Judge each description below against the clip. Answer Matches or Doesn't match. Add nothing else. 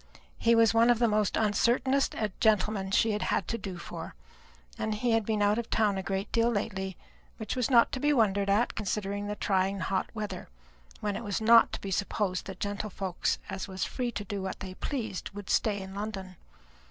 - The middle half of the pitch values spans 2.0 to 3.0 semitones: Matches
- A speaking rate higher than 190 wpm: Matches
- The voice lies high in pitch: Matches